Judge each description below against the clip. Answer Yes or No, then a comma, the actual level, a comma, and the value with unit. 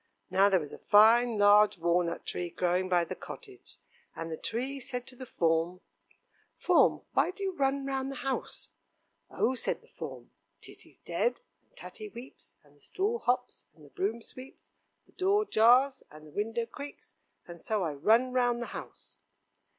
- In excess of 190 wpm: No, average, 175 wpm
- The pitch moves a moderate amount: No, wide, 7.0 semitones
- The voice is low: No, high, 230 Hz